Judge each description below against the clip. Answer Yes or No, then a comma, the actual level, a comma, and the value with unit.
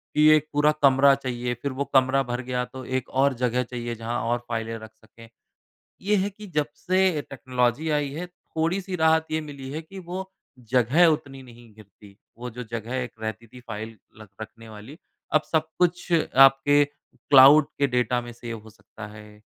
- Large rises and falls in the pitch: No, average, 4.6 semitones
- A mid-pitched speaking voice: No, low, 130 Hz